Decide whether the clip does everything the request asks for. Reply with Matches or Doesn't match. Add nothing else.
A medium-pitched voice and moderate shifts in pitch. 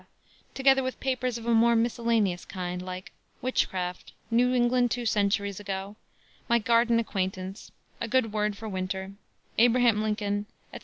Doesn't match